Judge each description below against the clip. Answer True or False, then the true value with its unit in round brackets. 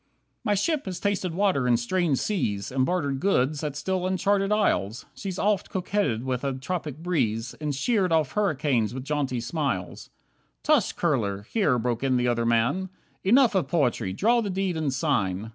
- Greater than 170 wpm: True (180 wpm)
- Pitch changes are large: True (7.3 semitones)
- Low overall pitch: False (150 Hz)